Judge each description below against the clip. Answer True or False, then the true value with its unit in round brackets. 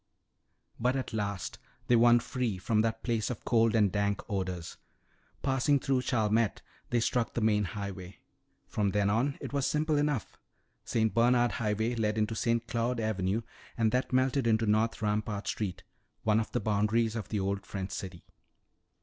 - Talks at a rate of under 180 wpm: True (165 wpm)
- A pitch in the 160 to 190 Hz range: False (110 Hz)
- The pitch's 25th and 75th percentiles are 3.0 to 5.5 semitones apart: False (2.6 semitones)